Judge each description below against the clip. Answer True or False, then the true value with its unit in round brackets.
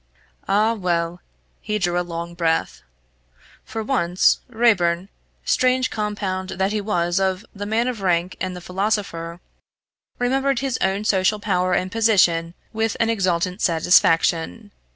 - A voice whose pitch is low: False (190 Hz)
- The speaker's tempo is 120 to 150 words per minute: True (135 wpm)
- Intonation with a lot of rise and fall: False (3.8 semitones)